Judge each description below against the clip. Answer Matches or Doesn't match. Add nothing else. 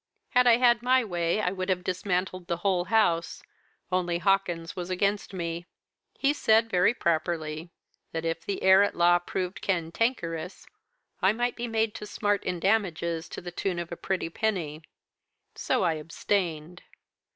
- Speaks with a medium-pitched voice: Matches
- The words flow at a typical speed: Matches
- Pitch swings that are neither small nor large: Matches